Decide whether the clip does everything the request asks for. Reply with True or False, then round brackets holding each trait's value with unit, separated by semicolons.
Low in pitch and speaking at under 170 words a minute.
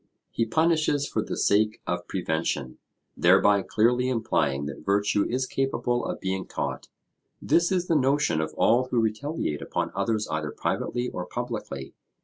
True (110 Hz; 150 wpm)